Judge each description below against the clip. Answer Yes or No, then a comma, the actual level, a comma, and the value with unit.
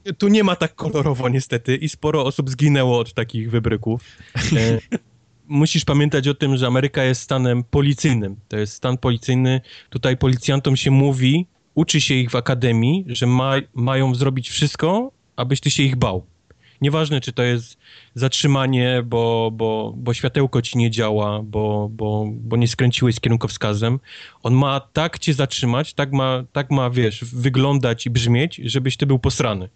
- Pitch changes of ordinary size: Yes, average, 3.2 semitones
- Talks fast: Yes, fast, 165 wpm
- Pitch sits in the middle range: No, low, 130 Hz